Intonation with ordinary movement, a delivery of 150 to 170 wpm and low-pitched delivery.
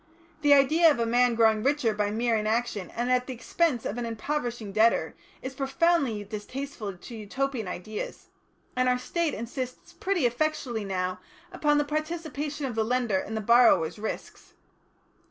No: average, 4.5 semitones; average, 160 wpm; high, 245 Hz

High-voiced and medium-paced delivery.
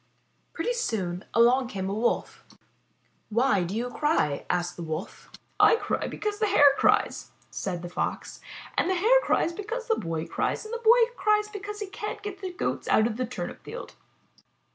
Yes: very high, 295 Hz; average, 185 wpm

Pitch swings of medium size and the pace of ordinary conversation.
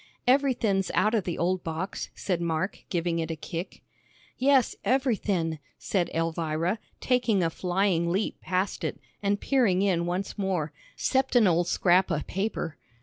Yes: average, 3.8 semitones; average, 150 wpm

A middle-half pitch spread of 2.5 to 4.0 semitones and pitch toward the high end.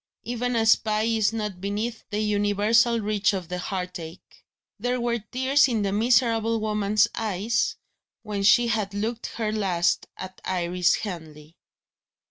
Yes: average, 2.8 semitones; high, 210 Hz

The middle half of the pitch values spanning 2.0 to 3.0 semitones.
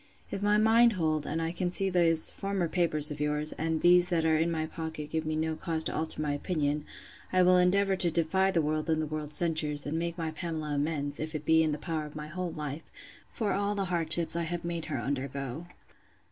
Yes: narrow, 2.4 semitones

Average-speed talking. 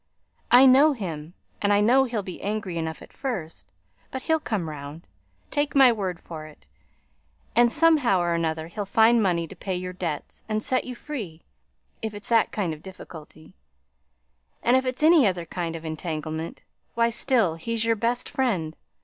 Yes: average, 175 wpm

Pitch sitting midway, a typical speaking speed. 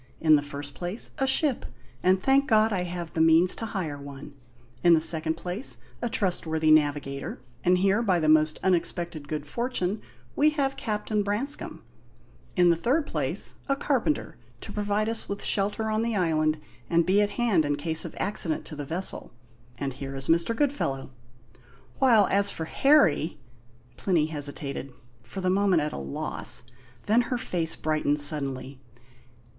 Yes: medium, 175 Hz; average, 165 wpm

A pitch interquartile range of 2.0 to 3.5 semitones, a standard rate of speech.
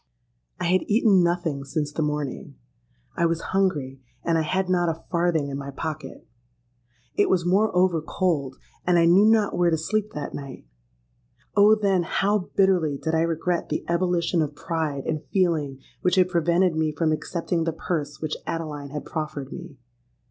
Yes: average, 3.2 semitones; average, 170 wpm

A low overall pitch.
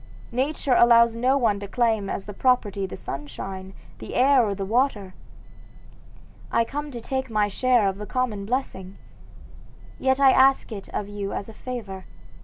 No: high, 230 Hz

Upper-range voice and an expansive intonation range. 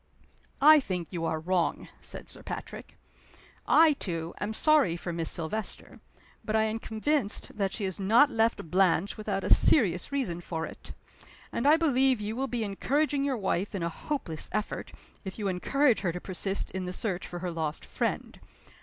Yes: high, 200 Hz; wide, 6.3 semitones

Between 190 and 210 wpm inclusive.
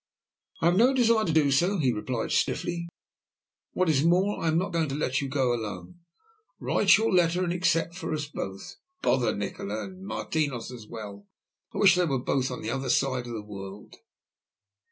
Yes: average, 195 wpm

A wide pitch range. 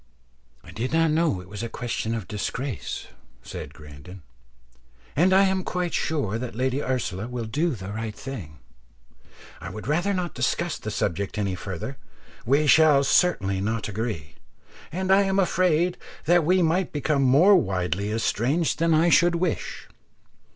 Yes: wide, 8.3 semitones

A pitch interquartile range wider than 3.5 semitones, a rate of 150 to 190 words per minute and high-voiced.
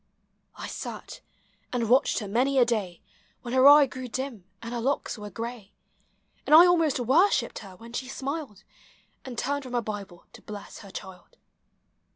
Yes: average, 4.4 semitones; average, 175 wpm; high, 245 Hz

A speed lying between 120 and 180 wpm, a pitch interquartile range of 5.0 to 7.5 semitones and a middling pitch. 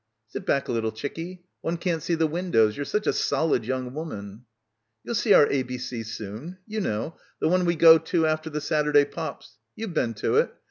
No: average, 200 wpm; wide, 5.4 semitones; medium, 150 Hz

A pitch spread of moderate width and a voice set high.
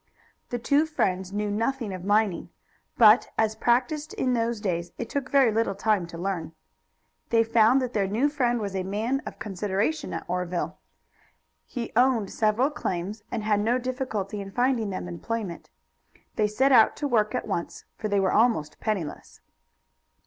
Yes: average, 4.0 semitones; high, 220 Hz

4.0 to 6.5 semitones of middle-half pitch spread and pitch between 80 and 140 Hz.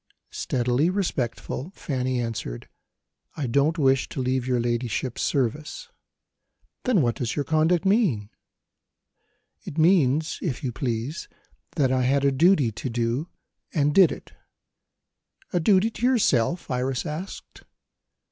Yes: average, 5.0 semitones; low, 135 Hz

